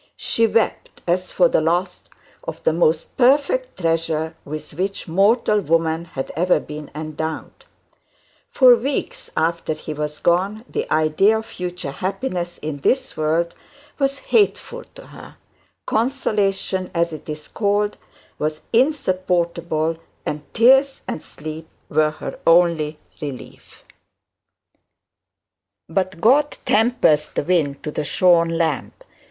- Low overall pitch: No, medium, 170 Hz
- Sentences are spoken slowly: Yes, slow, 125 wpm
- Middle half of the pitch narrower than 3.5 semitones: No, average, 5.2 semitones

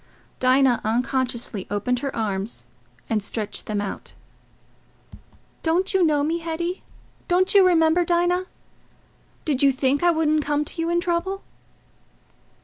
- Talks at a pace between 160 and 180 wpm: No, slow, 135 wpm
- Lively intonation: Yes, wide, 5.7 semitones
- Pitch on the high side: Yes, very high, 300 Hz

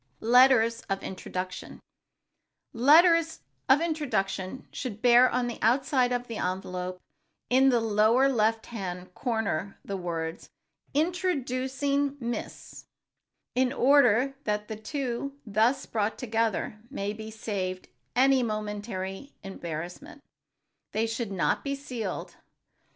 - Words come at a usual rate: No, slow, 120 wpm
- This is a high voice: Yes, high, 230 Hz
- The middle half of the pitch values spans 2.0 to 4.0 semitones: No, average, 4.7 semitones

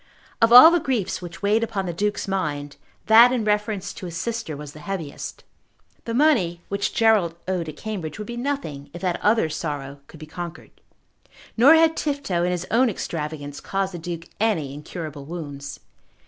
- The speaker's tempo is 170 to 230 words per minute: Yes, average, 180 wpm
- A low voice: No, medium, 185 Hz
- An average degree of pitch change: No, wide, 6.2 semitones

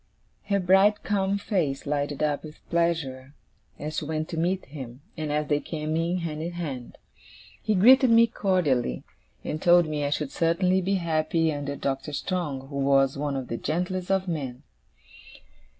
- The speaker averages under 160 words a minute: No, average, 170 wpm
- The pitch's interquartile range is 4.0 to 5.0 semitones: Yes, average, 4.3 semitones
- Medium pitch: Yes, medium, 155 Hz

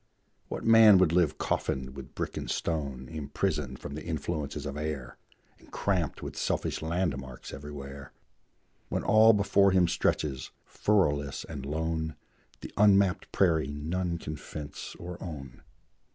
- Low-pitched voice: Yes, very low, 80 Hz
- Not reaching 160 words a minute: Yes, average, 140 wpm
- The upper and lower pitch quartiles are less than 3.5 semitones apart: No, average, 4.2 semitones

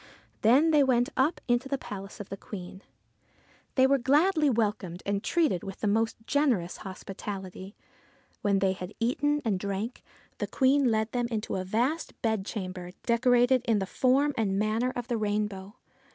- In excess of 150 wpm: Yes, average, 165 wpm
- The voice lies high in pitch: Yes, high, 225 Hz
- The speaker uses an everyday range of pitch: Yes, average, 4.8 semitones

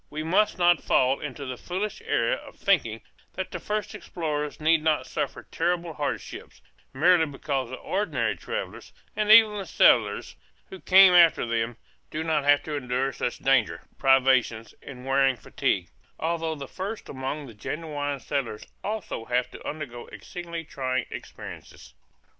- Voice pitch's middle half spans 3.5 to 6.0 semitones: Yes, average, 4.8 semitones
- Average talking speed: Yes, average, 155 wpm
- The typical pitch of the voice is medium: Yes, medium, 150 Hz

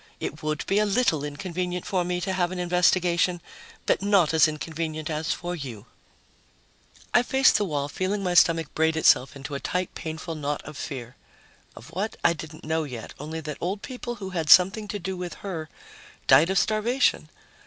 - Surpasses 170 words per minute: Yes, average, 185 wpm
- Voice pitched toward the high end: No, medium, 170 Hz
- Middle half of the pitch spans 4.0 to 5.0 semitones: No, average, 3.5 semitones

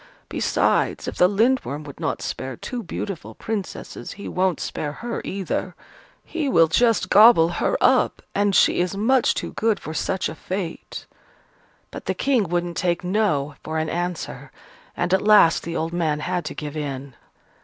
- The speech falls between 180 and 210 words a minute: No, average, 170 wpm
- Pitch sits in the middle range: Yes, medium, 180 Hz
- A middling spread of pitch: Yes, average, 4.7 semitones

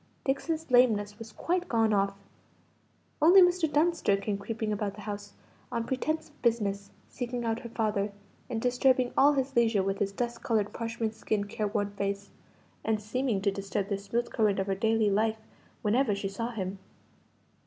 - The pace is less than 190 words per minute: Yes, average, 170 wpm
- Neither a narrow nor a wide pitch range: Yes, average, 3.5 semitones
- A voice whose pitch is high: Yes, high, 220 Hz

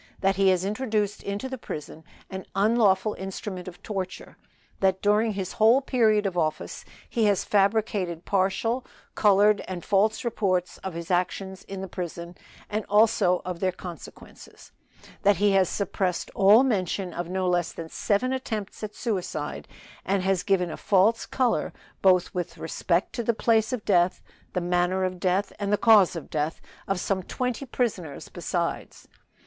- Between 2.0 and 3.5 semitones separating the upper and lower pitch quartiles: Yes, average, 2.8 semitones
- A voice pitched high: Yes, high, 195 Hz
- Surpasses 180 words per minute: No, average, 165 wpm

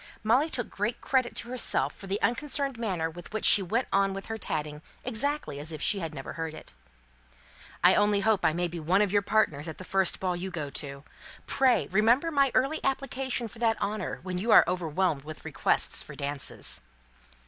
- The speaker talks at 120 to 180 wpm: No, fast, 205 wpm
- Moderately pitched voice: No, high, 195 Hz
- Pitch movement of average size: No, wide, 6.3 semitones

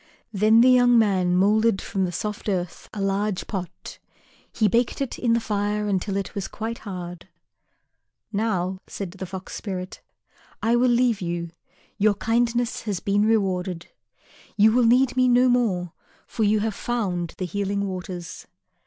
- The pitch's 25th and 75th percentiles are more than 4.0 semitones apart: No, average, 3.6 semitones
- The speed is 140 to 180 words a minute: Yes, average, 160 wpm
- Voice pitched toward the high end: Yes, high, 205 Hz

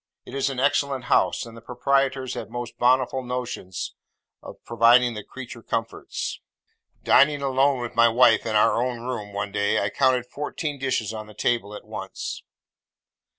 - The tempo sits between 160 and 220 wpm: Yes, average, 165 wpm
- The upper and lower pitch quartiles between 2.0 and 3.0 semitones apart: Yes, narrow, 2.6 semitones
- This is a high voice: No, low, 125 Hz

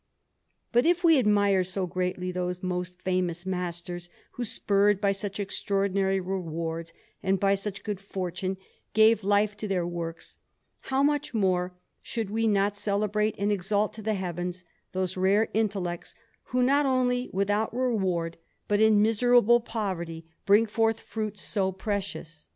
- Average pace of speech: Yes, average, 145 wpm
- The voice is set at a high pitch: Yes, high, 200 Hz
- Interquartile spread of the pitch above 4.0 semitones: No, average, 3.0 semitones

